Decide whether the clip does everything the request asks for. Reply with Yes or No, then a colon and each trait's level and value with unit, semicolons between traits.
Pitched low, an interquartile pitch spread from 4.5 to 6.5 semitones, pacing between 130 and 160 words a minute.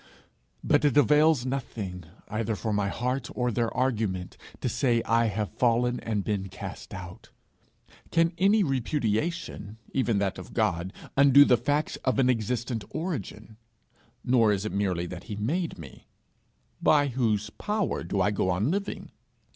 Yes: low, 115 Hz; average, 5.0 semitones; average, 155 wpm